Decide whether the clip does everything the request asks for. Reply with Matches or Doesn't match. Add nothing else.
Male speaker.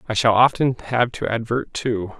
Matches